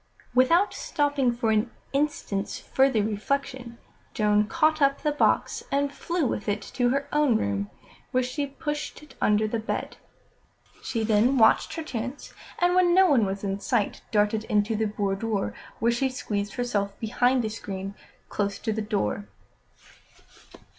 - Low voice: No, high, 235 Hz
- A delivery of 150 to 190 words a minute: Yes, average, 155 wpm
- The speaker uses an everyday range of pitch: Yes, average, 5.0 semitones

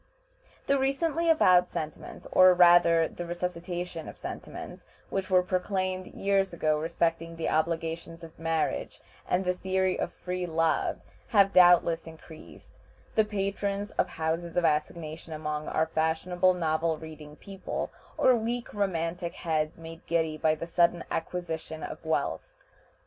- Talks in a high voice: No, medium, 170 Hz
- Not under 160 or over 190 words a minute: No, average, 140 wpm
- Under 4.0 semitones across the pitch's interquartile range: Yes, narrow, 2.5 semitones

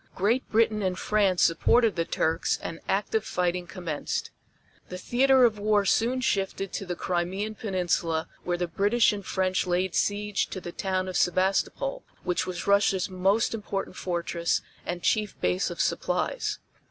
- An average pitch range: Yes, average, 3.0 semitones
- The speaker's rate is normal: Yes, average, 155 wpm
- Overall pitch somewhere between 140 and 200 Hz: Yes, high, 190 Hz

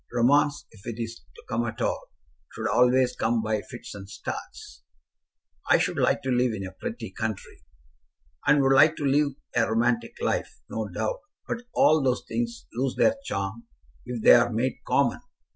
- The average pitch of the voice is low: Yes, low, 120 Hz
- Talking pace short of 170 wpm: No, average, 175 wpm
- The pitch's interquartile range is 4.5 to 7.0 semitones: No, average, 3.4 semitones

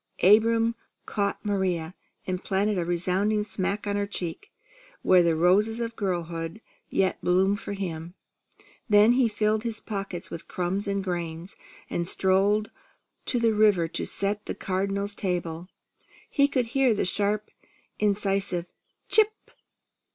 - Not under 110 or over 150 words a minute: Yes, slow, 135 wpm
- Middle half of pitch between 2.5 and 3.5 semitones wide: Yes, average, 2.9 semitones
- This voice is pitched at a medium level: No, high, 200 Hz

